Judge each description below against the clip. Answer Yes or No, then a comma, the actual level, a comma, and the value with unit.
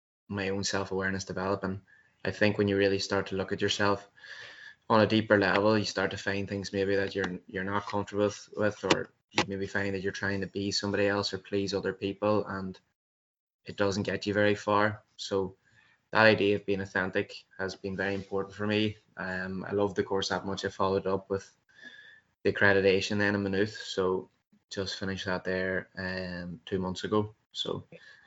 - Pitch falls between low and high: No, low, 100 Hz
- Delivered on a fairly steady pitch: Yes, narrow, 1.1 semitones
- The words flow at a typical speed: Yes, average, 190 wpm